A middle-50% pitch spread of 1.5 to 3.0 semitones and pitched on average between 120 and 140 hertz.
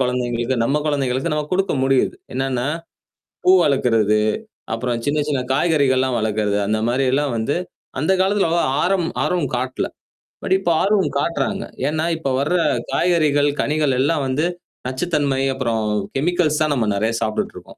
No: average, 3.9 semitones; low, 135 Hz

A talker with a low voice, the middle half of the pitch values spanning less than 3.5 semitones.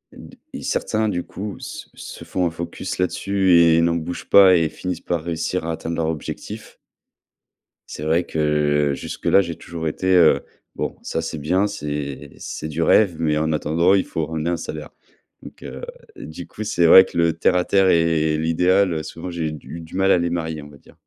Yes: very low, 85 Hz; narrow, 2.5 semitones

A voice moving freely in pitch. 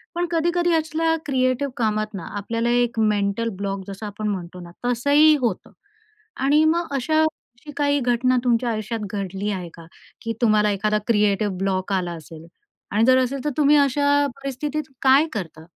Yes: wide, 6.0 semitones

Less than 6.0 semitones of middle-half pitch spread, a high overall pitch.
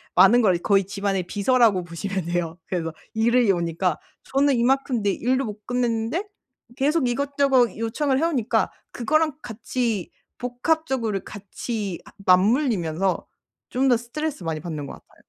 Yes: wide, 5.5 semitones; high, 225 Hz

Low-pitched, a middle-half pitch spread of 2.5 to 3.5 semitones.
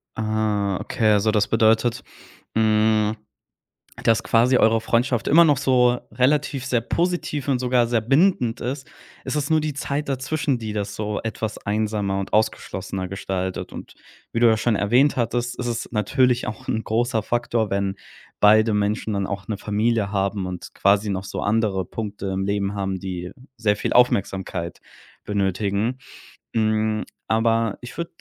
Yes: low, 110 Hz; average, 3.2 semitones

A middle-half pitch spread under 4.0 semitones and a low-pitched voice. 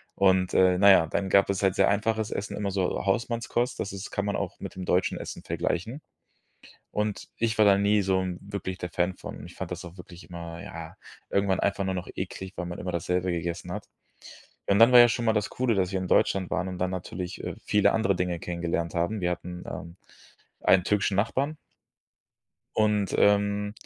Yes: narrow, 2.4 semitones; very low, 95 Hz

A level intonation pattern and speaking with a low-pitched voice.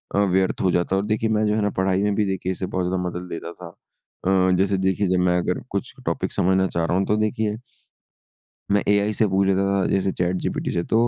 Yes: narrow, 1.9 semitones; very low, 95 Hz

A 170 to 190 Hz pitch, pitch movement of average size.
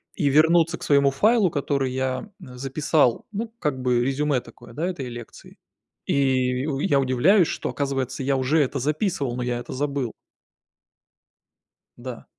No: low, 135 Hz; average, 3.0 semitones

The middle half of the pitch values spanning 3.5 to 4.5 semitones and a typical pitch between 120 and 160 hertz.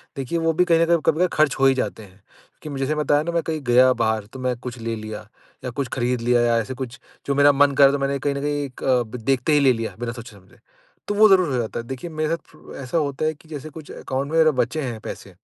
Yes: average, 4.2 semitones; low, 135 Hz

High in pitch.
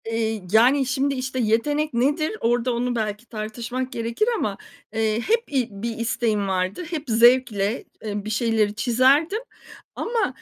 Yes: high, 235 Hz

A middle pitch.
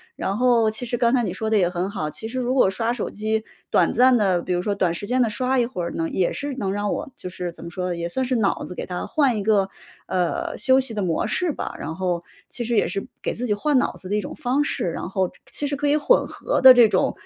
No: high, 220 Hz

